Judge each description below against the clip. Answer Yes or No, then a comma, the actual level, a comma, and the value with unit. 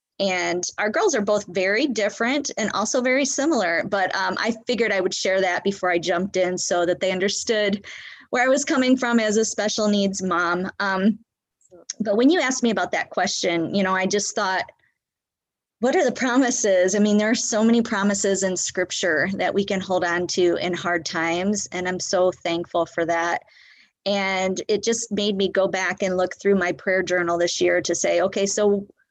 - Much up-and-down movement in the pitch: No, average, 3.0 semitones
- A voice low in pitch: No, high, 195 Hz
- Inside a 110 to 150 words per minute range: No, average, 200 wpm